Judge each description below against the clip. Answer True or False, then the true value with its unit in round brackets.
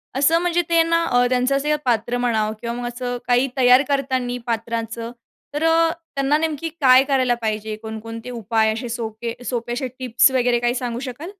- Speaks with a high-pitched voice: True (245 Hz)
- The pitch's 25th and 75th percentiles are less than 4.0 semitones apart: True (2.9 semitones)